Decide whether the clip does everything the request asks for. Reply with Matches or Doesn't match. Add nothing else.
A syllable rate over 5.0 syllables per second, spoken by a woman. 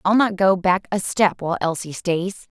Doesn't match